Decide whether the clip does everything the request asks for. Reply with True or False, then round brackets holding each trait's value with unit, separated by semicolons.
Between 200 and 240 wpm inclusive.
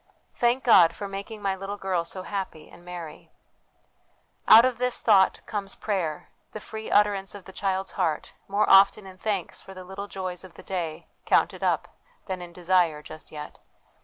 False (190 wpm)